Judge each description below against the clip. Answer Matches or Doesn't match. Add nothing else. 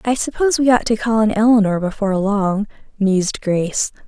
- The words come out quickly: Doesn't match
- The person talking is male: Doesn't match